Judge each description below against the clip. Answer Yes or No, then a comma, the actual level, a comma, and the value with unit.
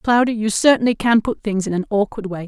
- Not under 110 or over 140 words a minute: No, fast, 240 wpm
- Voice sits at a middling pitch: No, high, 215 Hz